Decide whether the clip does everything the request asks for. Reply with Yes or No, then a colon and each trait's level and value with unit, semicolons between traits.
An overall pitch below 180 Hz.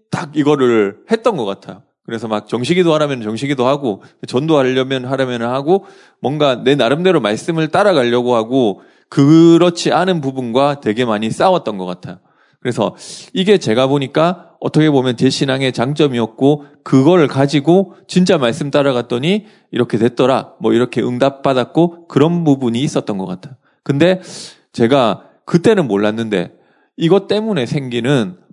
Yes: medium, 140 Hz